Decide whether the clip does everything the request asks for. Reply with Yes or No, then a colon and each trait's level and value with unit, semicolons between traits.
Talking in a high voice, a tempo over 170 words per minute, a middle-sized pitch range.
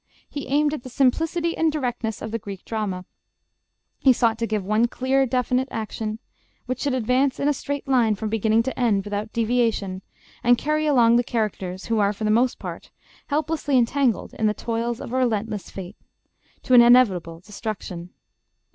Yes: high, 235 Hz; average, 180 wpm; average, 3.4 semitones